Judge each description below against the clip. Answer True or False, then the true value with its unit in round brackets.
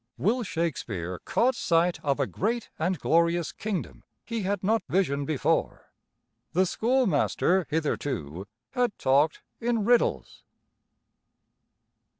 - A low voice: False (175 Hz)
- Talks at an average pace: False (110 wpm)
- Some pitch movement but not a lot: False (7.1 semitones)